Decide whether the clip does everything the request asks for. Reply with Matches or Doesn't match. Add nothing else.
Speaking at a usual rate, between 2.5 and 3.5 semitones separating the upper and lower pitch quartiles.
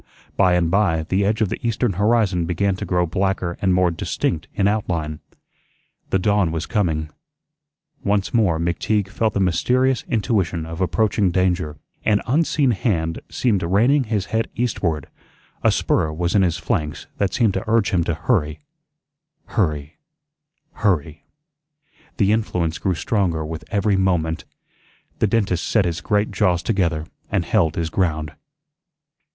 Doesn't match